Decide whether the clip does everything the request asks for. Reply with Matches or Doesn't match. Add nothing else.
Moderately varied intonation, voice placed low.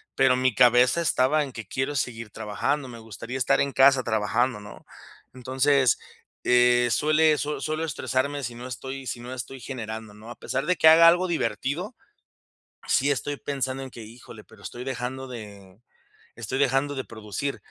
Matches